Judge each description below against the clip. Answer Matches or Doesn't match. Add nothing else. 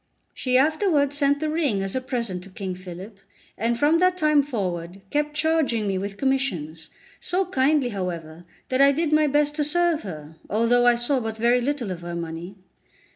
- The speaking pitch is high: Matches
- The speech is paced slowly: Doesn't match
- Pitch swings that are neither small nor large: Doesn't match